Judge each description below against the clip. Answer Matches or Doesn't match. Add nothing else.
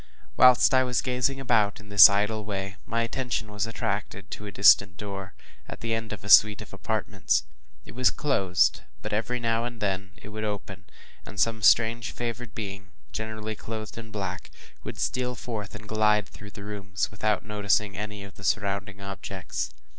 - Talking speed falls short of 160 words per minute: Doesn't match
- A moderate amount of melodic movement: Doesn't match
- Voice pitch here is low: Matches